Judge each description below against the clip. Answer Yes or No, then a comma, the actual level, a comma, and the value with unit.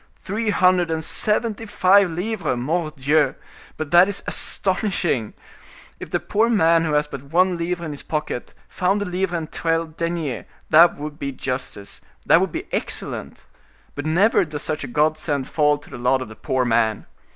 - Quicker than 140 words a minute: Yes, average, 175 wpm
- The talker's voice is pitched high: No, medium, 160 Hz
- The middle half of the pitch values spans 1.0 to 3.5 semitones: No, average, 4.1 semitones